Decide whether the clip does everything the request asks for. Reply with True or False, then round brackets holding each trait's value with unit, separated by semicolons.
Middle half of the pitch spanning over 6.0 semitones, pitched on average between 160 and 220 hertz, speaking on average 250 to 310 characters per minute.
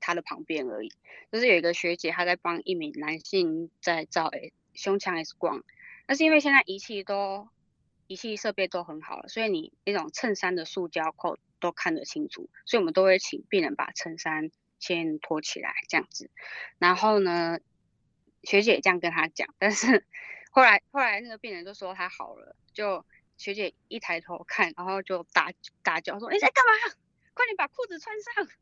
True (6.5 semitones; 190 Hz; 270 characters per minute)